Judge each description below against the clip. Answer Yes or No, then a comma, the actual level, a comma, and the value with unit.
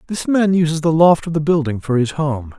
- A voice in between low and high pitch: Yes, medium, 155 Hz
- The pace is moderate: No, fast, 255 wpm